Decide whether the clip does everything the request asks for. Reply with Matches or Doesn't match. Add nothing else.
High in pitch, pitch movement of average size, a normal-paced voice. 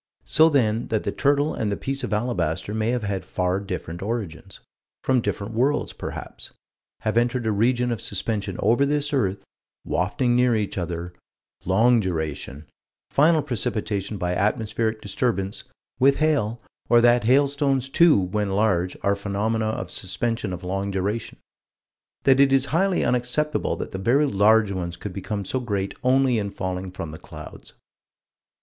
Doesn't match